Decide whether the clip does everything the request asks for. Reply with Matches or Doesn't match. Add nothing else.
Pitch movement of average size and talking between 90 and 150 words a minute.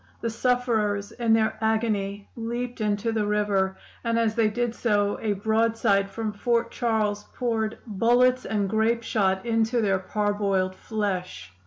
Doesn't match